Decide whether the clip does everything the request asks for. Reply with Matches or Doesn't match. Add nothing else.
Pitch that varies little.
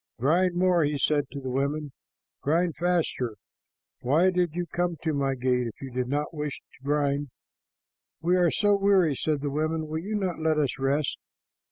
Doesn't match